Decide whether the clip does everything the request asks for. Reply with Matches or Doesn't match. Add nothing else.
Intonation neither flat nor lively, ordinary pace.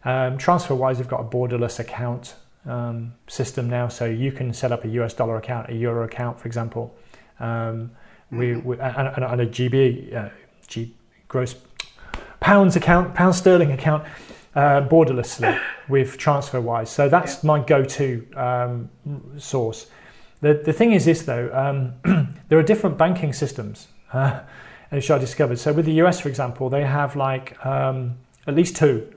Matches